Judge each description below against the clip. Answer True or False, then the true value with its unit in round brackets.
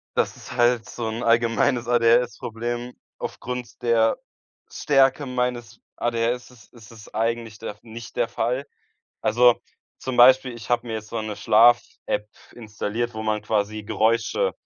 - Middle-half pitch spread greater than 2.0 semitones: False (1.6 semitones)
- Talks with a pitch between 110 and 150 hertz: True (115 Hz)